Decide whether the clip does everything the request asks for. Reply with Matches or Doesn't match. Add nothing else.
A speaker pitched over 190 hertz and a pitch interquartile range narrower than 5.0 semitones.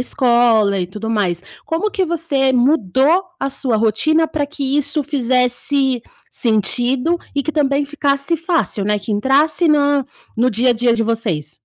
Matches